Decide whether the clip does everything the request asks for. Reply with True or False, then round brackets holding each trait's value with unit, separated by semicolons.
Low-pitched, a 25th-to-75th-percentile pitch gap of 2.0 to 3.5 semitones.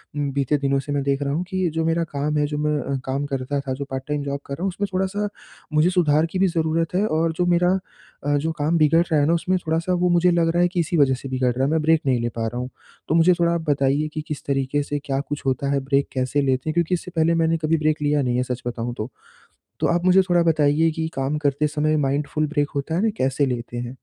False (150 Hz; 3.2 semitones)